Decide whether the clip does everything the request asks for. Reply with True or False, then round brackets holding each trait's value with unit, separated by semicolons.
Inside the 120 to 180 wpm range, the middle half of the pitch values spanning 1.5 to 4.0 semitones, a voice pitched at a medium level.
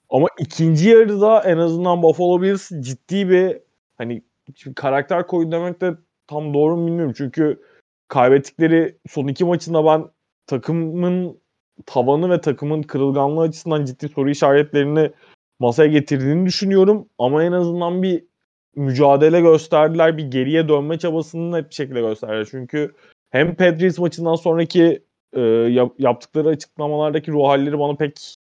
True (135 wpm; 3.3 semitones; 155 Hz)